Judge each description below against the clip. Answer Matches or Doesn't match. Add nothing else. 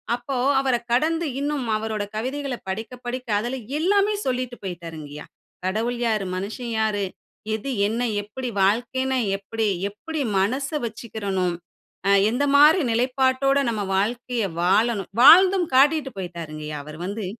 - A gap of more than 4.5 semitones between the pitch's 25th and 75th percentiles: Matches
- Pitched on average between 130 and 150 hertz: Doesn't match